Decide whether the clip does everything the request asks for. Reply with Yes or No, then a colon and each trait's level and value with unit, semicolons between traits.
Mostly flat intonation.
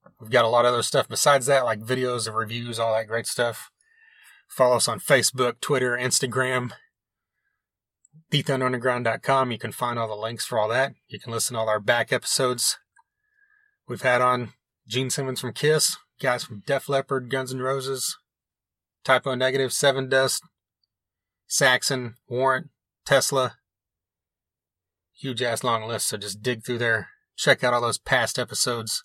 No: average, 3.0 semitones